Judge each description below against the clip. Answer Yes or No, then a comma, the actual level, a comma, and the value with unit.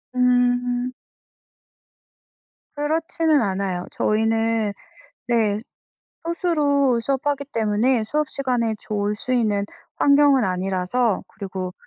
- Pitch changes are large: No, average, 5.0 semitones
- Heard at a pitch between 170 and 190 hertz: No, high, 240 Hz